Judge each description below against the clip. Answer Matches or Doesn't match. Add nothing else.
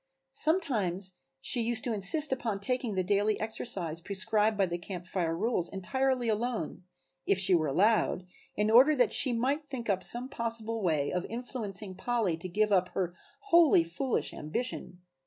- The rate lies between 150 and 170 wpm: Matches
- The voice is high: Matches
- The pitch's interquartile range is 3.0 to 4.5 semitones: Doesn't match